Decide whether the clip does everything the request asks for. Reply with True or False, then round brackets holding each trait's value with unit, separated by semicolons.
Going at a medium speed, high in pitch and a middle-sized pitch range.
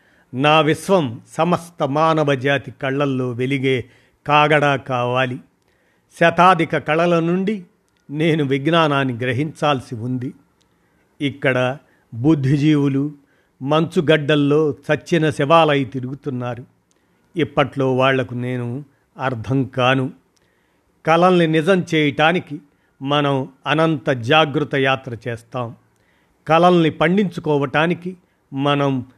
False (80 wpm; 145 Hz; 3.3 semitones)